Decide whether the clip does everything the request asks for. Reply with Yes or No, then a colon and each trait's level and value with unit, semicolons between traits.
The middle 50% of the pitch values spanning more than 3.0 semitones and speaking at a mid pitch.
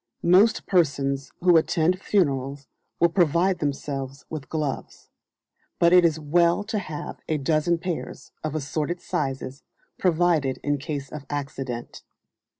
Yes: average, 3.9 semitones; medium, 155 Hz